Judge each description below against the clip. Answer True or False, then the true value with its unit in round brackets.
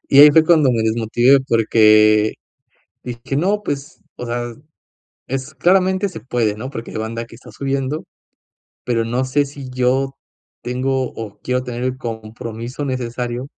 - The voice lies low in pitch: True (125 Hz)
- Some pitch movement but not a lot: True (3.0 semitones)